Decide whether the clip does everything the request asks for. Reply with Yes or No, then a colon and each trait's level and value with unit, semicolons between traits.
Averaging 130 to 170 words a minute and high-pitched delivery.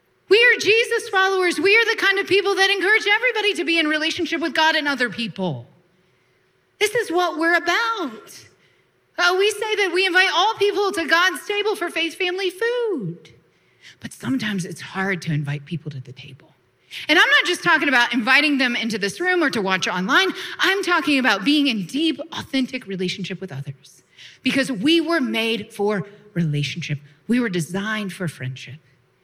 No: average, 180 wpm; very high, 285 Hz